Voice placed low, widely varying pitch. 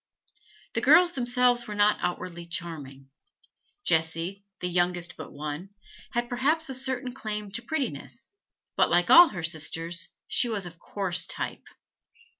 No: high, 190 Hz; wide, 6.3 semitones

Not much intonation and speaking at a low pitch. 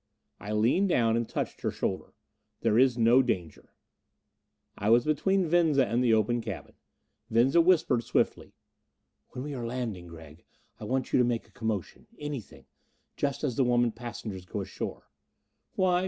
No: average, 3.8 semitones; low, 120 Hz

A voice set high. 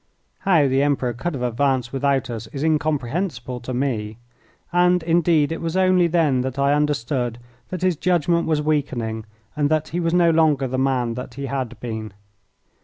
No: medium, 140 Hz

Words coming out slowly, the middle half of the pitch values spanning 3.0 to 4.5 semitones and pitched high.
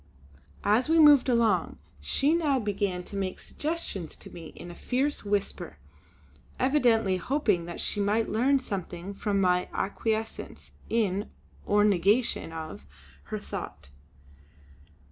No: slow, 125 wpm; wide, 5.4 semitones; high, 205 Hz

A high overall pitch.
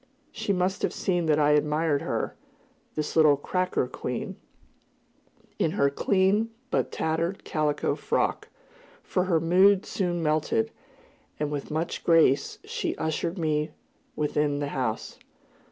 No: medium, 160 Hz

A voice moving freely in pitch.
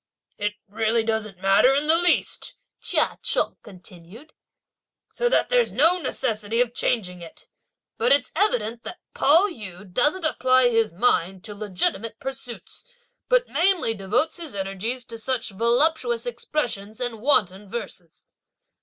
Yes: wide, 5.9 semitones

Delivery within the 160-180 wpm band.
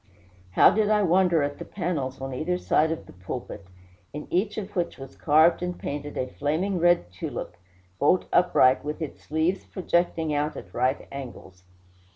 Yes: average, 175 wpm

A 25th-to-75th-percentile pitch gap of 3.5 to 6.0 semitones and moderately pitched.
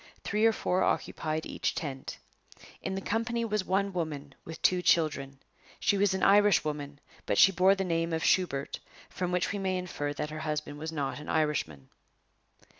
Yes: average, 4.4 semitones; medium, 165 Hz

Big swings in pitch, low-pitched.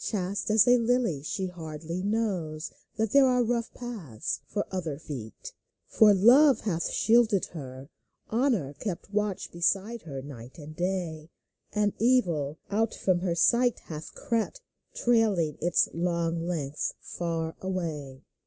No: wide, 6.1 semitones; medium, 180 Hz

